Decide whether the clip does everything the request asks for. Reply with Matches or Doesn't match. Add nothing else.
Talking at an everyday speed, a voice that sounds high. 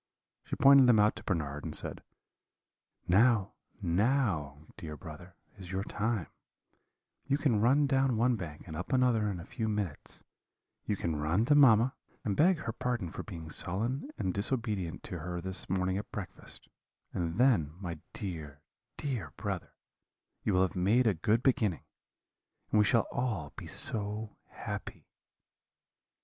Doesn't match